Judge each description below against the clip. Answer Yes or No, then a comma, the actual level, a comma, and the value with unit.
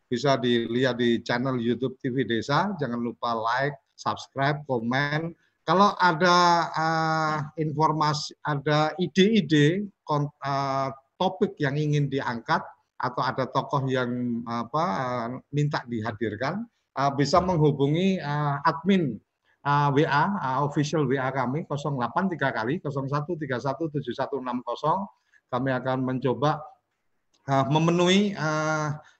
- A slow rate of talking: No, average, 105 wpm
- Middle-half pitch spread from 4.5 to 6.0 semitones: No, average, 3.4 semitones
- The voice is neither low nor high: Yes, medium, 145 Hz